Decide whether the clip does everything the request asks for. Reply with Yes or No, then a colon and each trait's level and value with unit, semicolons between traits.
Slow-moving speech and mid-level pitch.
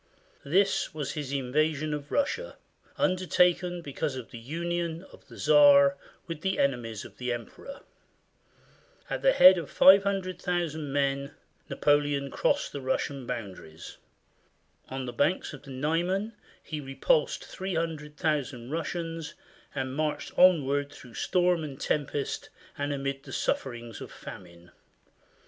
Yes: slow, 130 wpm; medium, 150 Hz